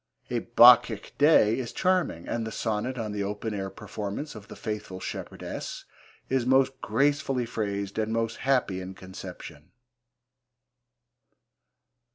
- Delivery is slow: Yes, slow, 130 wpm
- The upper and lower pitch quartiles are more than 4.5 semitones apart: No, average, 4.1 semitones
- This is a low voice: Yes, low, 110 Hz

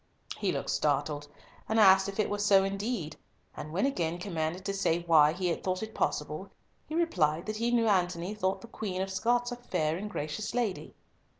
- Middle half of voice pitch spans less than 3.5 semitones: No, average, 4.3 semitones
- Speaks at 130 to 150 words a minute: No, average, 200 wpm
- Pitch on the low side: No, high, 190 Hz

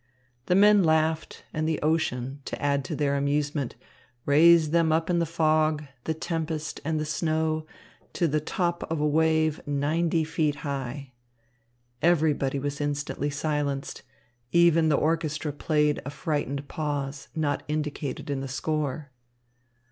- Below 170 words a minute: Yes, average, 140 wpm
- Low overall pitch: No, medium, 155 Hz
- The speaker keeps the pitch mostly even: Yes, narrow, 2.0 semitones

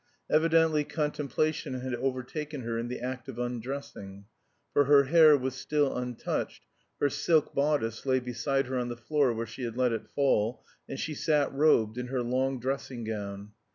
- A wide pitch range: No, average, 3.1 semitones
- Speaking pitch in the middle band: No, low, 130 Hz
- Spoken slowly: No, average, 175 wpm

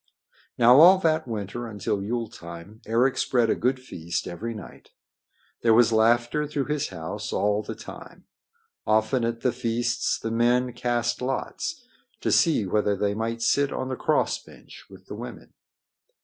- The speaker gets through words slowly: No, average, 165 wpm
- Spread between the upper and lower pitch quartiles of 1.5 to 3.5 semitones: Yes, average, 3.0 semitones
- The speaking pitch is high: No, low, 115 Hz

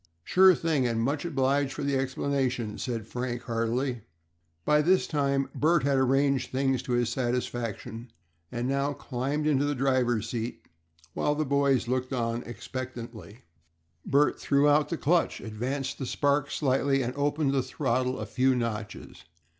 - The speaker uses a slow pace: No, average, 155 wpm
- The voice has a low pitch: Yes, low, 130 Hz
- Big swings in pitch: No, average, 2.7 semitones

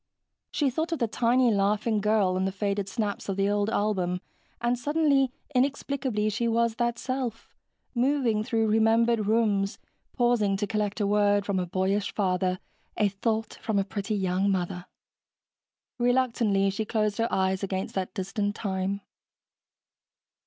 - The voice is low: No, high, 210 Hz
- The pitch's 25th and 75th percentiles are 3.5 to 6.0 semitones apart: No, average, 3.1 semitones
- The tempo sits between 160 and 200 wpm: No, average, 150 wpm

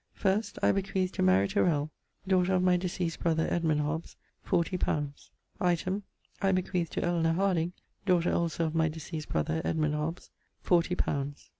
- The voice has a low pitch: No, medium, 170 Hz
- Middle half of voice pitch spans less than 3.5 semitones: Yes, average, 2.9 semitones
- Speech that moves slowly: No, average, 160 wpm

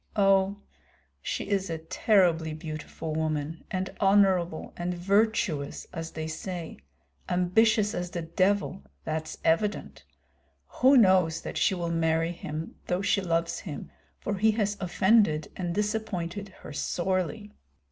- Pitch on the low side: No, medium, 180 Hz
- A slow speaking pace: Yes, slow, 130 wpm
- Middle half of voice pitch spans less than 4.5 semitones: Yes, average, 3.7 semitones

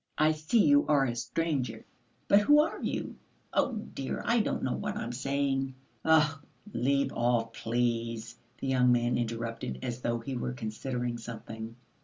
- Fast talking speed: No, average, 165 wpm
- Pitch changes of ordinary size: Yes, average, 3.6 semitones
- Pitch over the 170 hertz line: No, low, 125 Hz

